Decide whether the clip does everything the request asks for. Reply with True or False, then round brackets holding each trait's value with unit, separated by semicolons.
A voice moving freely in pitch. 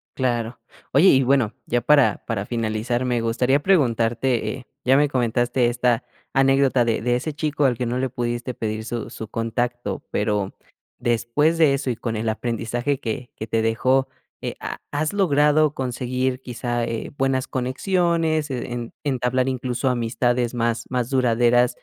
False (2.4 semitones)